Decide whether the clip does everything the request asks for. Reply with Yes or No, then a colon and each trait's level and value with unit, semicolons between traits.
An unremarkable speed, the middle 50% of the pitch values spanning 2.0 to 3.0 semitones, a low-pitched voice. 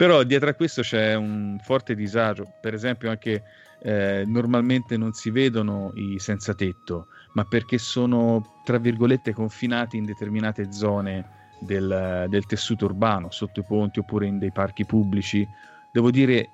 Yes: average, 150 wpm; narrow, 2.6 semitones; low, 105 Hz